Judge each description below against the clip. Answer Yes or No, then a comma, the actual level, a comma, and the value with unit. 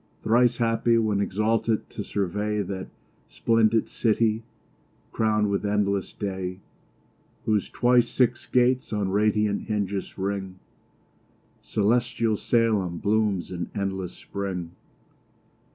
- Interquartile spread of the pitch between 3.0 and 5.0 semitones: No, narrow, 2.5 semitones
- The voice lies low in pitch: Yes, low, 105 Hz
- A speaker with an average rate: No, slow, 105 wpm